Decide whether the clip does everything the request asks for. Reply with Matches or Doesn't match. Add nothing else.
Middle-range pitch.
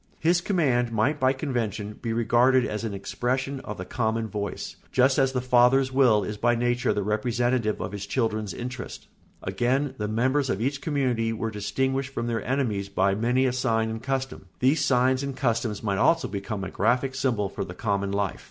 Doesn't match